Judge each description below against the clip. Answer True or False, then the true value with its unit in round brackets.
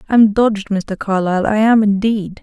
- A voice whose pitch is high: True (205 Hz)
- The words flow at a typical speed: True (175 wpm)